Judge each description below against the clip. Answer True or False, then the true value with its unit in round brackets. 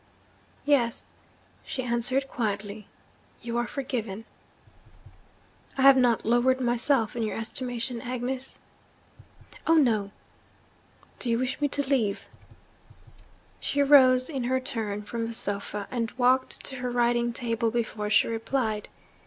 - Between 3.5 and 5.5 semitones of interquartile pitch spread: False (2.4 semitones)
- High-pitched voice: True (240 Hz)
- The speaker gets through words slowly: True (130 wpm)